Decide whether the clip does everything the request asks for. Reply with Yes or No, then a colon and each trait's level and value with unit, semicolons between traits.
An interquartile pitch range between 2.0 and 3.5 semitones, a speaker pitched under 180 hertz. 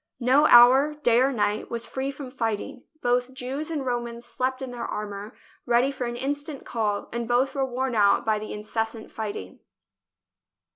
No: average, 2.9 semitones; high, 245 Hz